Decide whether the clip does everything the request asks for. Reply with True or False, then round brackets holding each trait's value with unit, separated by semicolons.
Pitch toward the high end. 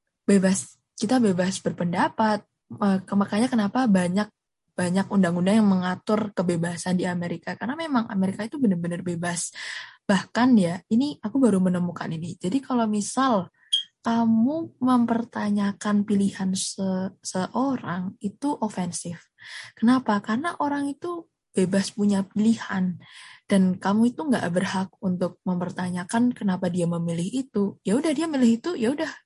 True (200 Hz)